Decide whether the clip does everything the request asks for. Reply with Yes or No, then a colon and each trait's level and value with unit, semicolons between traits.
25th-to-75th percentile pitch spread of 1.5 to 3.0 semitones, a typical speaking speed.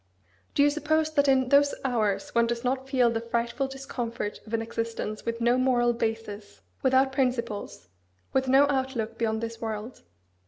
Yes: average, 2.7 semitones; average, 165 wpm